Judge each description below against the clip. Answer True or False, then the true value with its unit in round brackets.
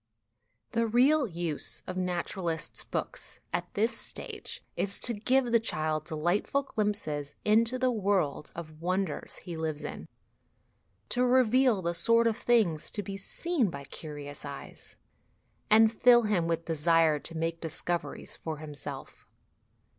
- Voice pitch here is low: False (185 Hz)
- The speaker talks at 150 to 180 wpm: False (140 wpm)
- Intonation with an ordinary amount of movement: False (6.3 semitones)